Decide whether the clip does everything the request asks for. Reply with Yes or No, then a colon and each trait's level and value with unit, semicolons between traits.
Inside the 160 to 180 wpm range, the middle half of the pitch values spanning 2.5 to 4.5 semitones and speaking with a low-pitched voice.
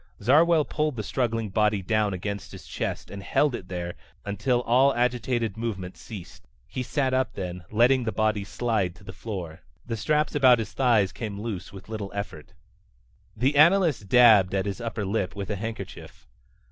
Yes: average, 175 wpm; average, 4.0 semitones; low, 110 Hz